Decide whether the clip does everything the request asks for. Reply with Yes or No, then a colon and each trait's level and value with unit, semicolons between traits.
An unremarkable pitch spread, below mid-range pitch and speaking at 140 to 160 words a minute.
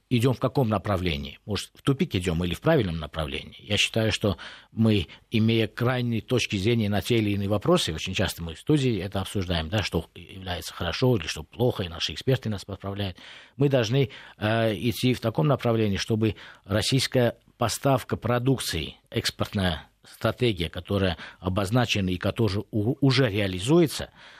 Yes: average, 4.6 semitones; low, 110 Hz; average, 155 wpm